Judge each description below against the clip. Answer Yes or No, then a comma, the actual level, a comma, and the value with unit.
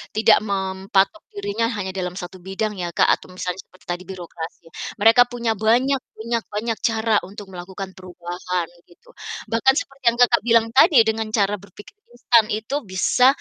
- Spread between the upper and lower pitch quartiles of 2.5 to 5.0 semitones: Yes, average, 3.6 semitones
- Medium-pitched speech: No, high, 205 Hz